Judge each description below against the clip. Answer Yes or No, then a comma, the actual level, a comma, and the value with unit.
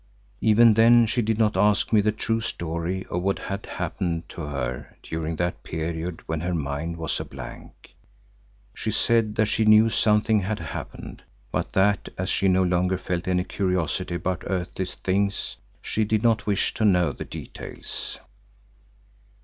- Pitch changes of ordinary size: Yes, average, 3.8 semitones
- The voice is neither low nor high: No, very low, 95 Hz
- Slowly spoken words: No, average, 165 wpm